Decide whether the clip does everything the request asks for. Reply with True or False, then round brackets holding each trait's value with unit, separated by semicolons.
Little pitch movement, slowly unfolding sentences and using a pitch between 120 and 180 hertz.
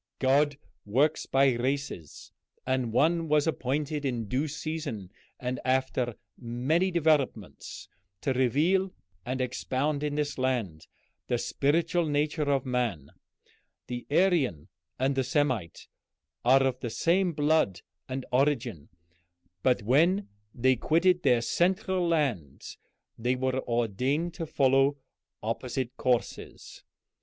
False (3.8 semitones; 115 wpm; 135 Hz)